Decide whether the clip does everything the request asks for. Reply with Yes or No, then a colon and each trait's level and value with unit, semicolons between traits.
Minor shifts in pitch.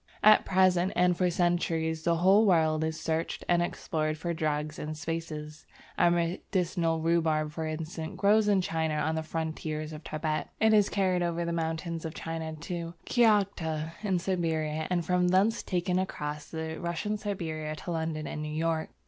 Yes: narrow, 2.2 semitones